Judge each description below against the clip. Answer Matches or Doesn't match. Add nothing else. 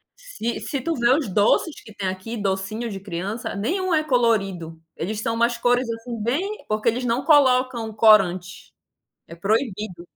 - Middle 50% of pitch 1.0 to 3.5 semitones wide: Doesn't match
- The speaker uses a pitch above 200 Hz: Matches